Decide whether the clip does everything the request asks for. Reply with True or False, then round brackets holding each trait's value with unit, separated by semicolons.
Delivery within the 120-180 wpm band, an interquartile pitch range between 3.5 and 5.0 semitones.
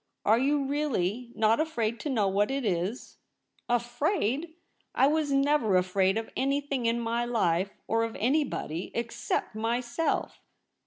True (150 wpm; 4.4 semitones)